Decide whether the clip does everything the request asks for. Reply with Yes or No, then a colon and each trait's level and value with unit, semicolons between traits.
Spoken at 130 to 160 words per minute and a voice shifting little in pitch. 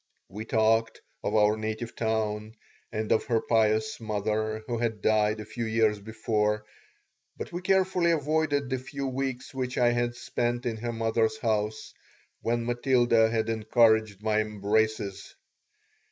Yes: average, 145 wpm; narrow, 1.9 semitones